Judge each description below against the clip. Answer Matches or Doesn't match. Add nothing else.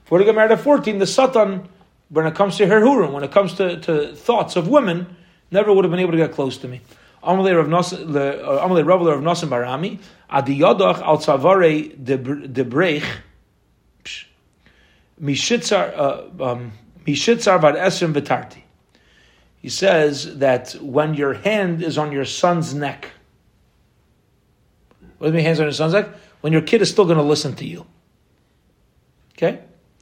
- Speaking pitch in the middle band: Matches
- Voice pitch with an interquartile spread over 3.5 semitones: Matches